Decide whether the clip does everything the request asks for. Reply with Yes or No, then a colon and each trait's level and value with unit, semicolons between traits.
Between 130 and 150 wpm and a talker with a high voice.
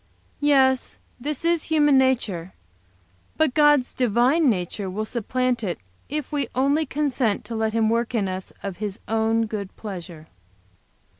Yes: average, 145 wpm; high, 235 Hz